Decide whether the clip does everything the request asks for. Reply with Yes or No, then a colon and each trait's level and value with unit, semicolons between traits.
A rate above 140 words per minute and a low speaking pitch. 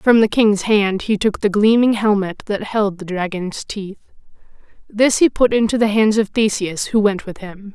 No: average, 200 wpm; high, 210 Hz